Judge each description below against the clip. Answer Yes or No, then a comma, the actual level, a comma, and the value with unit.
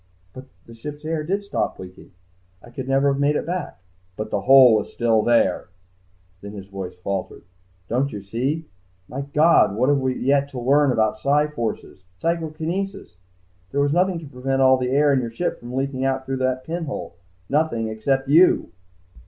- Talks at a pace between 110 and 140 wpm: No, average, 185 wpm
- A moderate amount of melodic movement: Yes, average, 4.4 semitones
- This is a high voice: No, low, 135 Hz